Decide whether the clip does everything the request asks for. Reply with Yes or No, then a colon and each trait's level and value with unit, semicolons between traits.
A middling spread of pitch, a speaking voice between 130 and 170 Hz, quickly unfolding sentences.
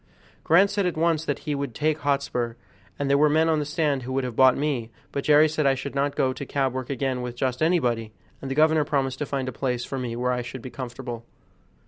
Yes: average, 3.1 semitones; low, 135 Hz; fast, 255 wpm